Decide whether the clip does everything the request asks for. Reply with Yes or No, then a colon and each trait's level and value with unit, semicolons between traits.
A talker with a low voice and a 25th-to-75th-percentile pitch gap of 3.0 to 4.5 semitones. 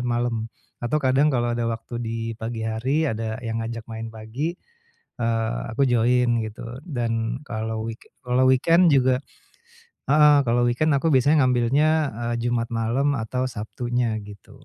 No: low, 120 Hz; narrow, 2.5 semitones